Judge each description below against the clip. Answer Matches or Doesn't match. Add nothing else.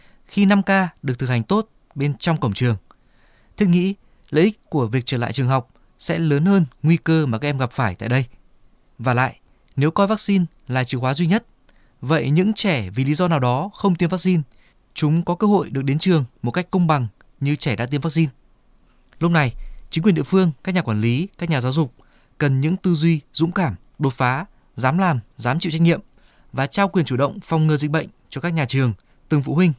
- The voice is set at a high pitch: Doesn't match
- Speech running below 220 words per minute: Doesn't match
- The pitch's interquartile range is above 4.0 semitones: Matches